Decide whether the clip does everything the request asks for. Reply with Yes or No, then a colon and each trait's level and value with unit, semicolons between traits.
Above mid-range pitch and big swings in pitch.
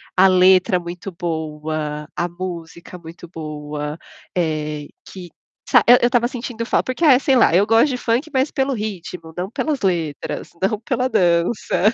No: medium, 180 Hz; wide, 6.1 semitones